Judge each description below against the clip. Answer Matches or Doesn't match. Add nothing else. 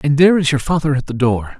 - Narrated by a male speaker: Matches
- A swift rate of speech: Matches